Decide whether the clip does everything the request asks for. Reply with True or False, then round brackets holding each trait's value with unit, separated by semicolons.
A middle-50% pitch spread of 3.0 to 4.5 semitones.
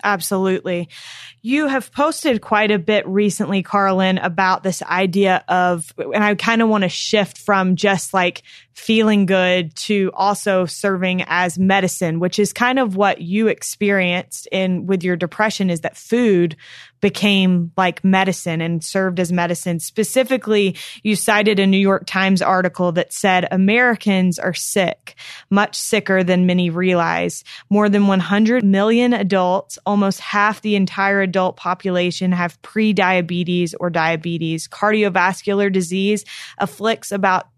False (2.4 semitones)